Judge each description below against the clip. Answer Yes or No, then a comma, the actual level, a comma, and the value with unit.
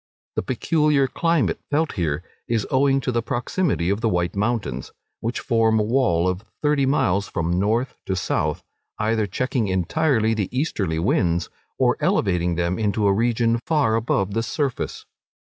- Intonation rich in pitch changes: Yes, wide, 5.8 semitones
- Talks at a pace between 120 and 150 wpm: No, average, 160 wpm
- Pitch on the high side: No, low, 110 Hz